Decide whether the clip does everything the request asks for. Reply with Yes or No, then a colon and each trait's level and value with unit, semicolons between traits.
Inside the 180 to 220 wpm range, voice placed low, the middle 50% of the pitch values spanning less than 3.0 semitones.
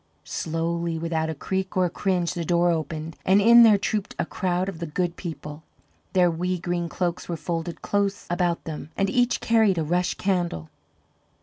No: average, 185 wpm; medium, 175 Hz; narrow, 2.4 semitones